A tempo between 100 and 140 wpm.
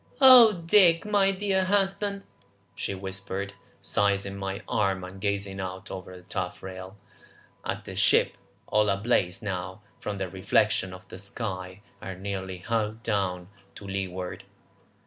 Yes: slow, 135 wpm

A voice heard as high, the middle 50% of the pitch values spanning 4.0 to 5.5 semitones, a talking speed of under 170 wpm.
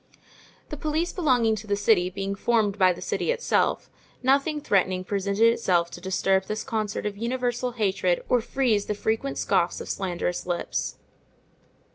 Yes: high, 210 Hz; average, 4.5 semitones; average, 155 wpm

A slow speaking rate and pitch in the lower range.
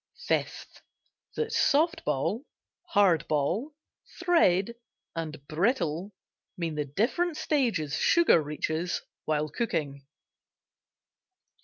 No: slow, 90 wpm; medium, 175 Hz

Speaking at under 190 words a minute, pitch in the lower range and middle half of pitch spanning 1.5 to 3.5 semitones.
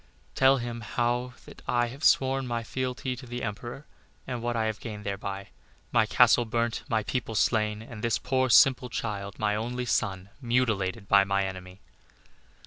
Yes: average, 165 wpm; low, 115 Hz; average, 3.1 semitones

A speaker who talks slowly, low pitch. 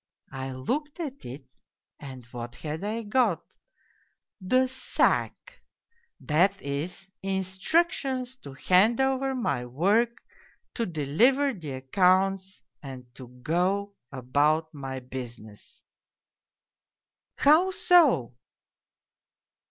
No: slow, 100 wpm; medium, 185 Hz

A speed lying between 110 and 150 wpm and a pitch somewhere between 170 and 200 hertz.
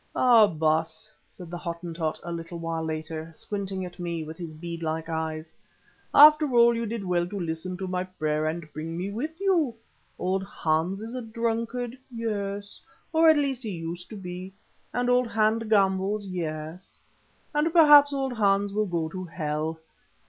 No: average, 170 wpm; medium, 185 Hz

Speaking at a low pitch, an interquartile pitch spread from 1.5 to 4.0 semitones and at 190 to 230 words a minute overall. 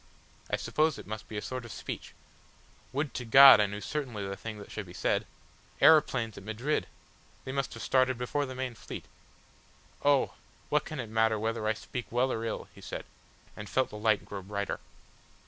Yes: low, 115 Hz; average, 3.6 semitones; average, 200 wpm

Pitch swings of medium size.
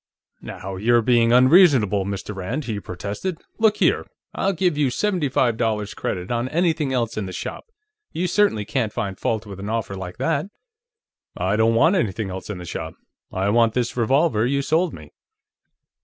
No: wide, 6.5 semitones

